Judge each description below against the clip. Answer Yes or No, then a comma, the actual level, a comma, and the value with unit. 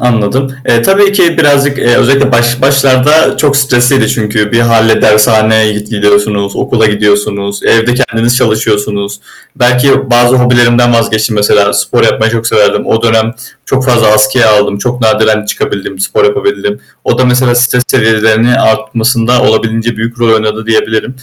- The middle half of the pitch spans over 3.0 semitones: No, average, 2.7 semitones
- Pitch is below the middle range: Yes, low, 115 Hz